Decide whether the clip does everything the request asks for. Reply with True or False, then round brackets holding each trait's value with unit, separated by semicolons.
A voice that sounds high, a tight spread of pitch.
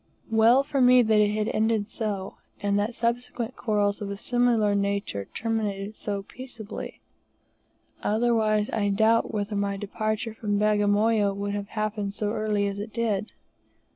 True (215 Hz; 1.8 semitones)